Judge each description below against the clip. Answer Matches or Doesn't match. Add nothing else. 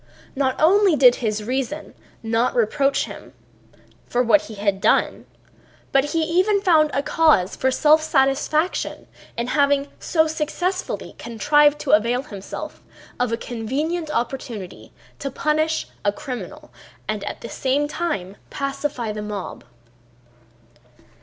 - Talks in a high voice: Matches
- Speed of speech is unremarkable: Doesn't match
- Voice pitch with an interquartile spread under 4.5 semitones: Doesn't match